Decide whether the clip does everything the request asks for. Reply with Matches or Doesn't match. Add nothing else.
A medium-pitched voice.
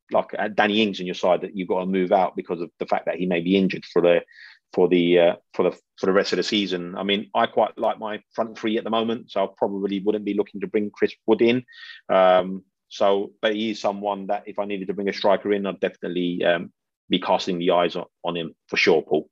Doesn't match